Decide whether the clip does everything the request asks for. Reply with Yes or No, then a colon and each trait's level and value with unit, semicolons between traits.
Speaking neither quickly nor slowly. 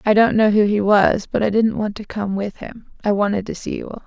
No: fast, 295 wpm